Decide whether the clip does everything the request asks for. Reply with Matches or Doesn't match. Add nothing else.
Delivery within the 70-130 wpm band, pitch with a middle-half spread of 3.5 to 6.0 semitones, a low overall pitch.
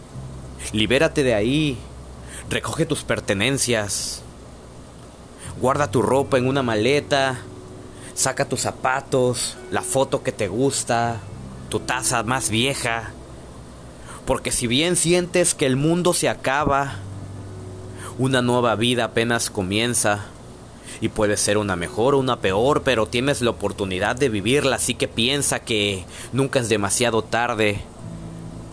Matches